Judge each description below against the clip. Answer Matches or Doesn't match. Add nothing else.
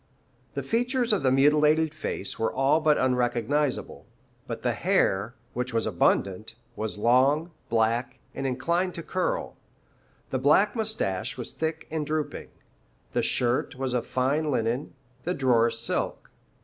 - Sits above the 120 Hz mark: Matches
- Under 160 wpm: Matches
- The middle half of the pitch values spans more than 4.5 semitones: Matches